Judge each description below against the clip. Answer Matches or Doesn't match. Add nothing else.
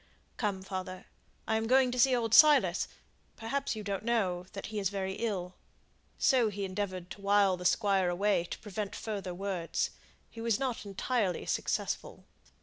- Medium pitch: Doesn't match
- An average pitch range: Matches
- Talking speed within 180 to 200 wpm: Doesn't match